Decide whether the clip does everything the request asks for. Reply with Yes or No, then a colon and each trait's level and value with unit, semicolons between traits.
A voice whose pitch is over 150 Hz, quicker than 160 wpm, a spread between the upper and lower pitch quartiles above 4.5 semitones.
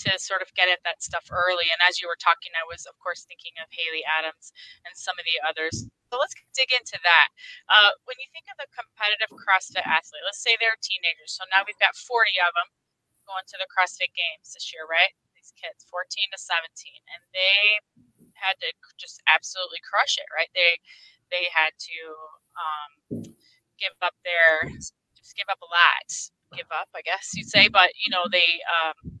Yes: medium, 185 Hz; average, 200 wpm; average, 5.3 semitones